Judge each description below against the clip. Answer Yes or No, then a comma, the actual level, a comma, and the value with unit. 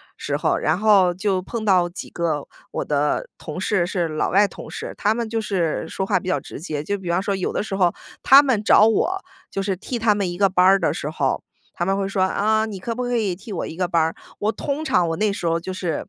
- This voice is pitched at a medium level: No, high, 195 Hz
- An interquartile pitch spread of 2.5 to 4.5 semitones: Yes, average, 3.4 semitones